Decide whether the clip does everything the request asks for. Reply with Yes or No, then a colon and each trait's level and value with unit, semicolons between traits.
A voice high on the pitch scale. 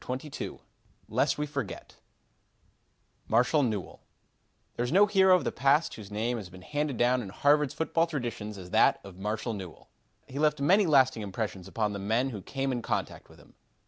No: low, 125 Hz